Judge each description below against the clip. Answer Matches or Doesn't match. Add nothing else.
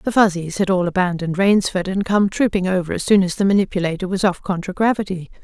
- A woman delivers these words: Matches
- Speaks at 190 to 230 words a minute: Matches